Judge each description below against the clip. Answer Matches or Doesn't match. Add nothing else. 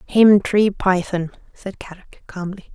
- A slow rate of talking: Matches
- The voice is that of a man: Doesn't match